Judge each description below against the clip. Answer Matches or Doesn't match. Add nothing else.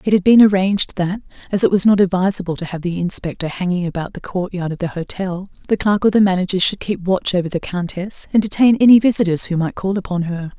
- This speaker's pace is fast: Matches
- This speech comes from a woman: Matches